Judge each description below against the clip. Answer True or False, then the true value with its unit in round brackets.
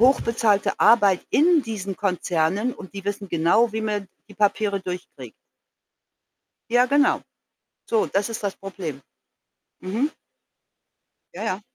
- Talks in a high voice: True (205 Hz)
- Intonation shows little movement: False (3.3 semitones)